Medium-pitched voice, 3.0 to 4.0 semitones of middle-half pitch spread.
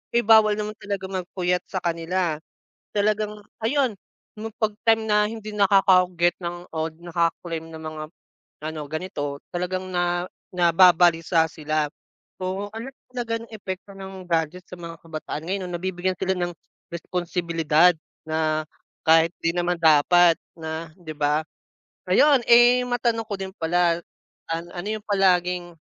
Yes: medium, 180 Hz; average, 3.3 semitones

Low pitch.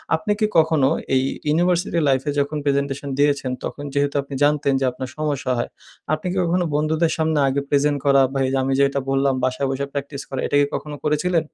No: medium, 145 Hz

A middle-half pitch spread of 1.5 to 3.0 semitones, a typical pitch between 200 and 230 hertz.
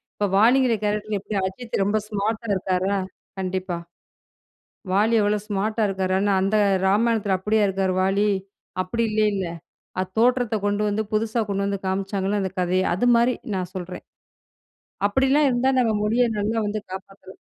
Yes: narrow, 2.5 semitones; high, 205 Hz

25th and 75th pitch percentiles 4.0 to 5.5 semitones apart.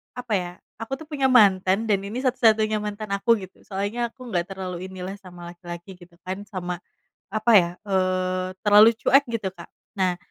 No: average, 3.1 semitones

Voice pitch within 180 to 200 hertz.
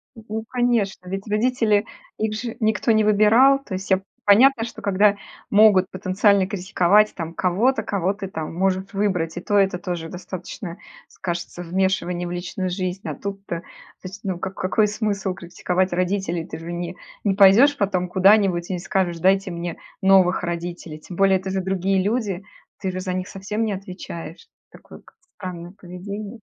Yes: high, 190 Hz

